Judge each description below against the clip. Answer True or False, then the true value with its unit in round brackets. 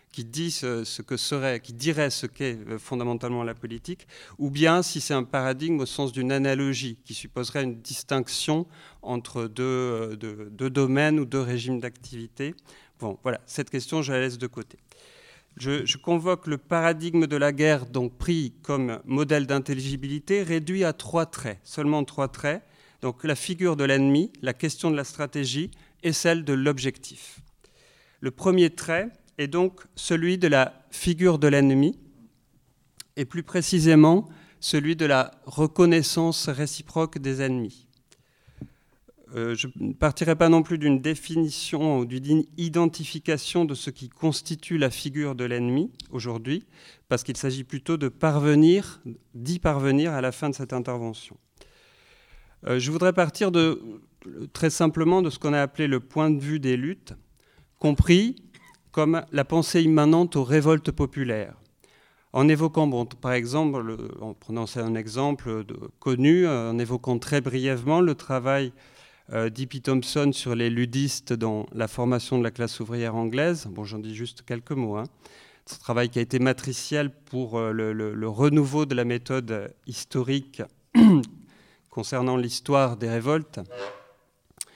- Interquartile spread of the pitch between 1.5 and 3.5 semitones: False (4.2 semitones)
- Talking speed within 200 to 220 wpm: False (155 wpm)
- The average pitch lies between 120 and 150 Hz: True (140 Hz)